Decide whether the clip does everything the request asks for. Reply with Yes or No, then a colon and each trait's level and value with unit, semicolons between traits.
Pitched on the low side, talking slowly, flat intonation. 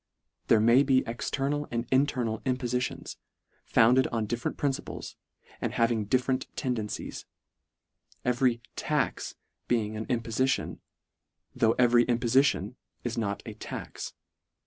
Yes: low, 120 Hz; slow, 130 wpm; narrow, 2.2 semitones